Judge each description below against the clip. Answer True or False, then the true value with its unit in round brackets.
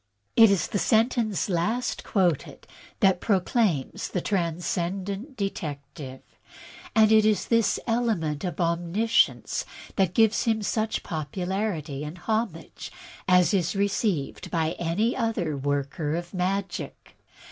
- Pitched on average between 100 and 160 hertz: False (190 Hz)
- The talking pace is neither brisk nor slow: False (120 wpm)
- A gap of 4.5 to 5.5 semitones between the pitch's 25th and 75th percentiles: True (4.8 semitones)